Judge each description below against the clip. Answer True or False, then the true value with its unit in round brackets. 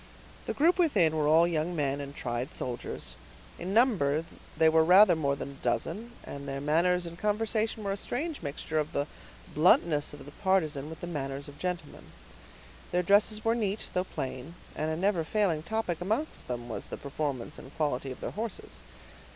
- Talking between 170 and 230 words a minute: True (185 wpm)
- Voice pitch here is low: False (165 Hz)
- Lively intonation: True (5.8 semitones)